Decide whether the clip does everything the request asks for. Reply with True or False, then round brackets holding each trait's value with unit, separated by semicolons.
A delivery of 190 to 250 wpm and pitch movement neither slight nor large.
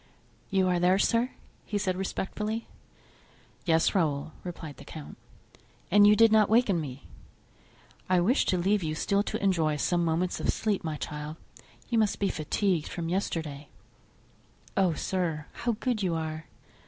False (155 wpm; 4.4 semitones)